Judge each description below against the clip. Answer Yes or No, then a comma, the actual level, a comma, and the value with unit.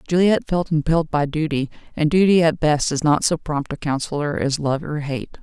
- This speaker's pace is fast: Yes, fast, 210 wpm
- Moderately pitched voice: Yes, medium, 155 Hz